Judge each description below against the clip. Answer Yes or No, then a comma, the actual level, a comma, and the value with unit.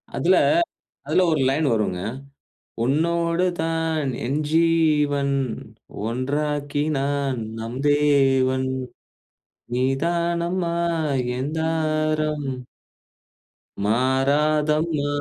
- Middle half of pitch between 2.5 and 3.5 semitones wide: Yes, average, 3.2 semitones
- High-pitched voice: No, medium, 150 Hz